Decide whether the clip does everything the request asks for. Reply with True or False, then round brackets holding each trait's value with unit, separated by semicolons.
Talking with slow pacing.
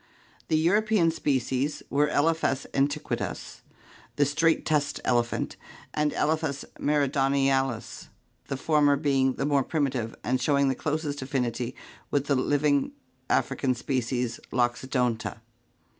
True (115 wpm)